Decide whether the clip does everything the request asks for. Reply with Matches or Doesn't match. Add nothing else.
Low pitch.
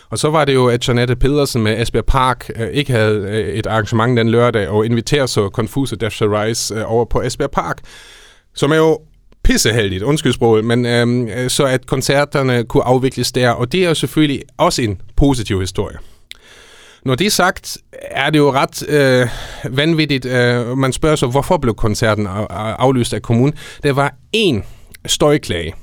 Matches